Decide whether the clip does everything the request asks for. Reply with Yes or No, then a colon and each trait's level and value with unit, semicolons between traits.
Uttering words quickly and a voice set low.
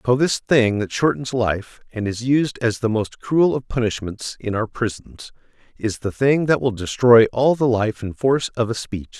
Yes: fast, 210 wpm; low, 120 Hz